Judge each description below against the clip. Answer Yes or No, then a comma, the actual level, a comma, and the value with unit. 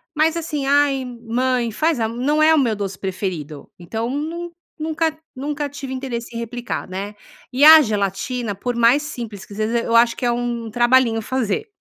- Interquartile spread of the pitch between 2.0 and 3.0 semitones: No, average, 4.3 semitones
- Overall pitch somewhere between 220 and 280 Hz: Yes, high, 245 Hz